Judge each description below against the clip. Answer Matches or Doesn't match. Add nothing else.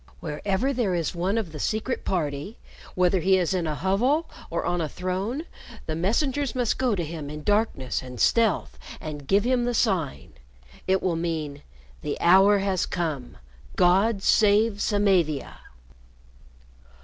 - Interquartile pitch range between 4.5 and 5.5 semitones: Matches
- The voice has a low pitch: Doesn't match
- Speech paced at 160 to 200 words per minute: Doesn't match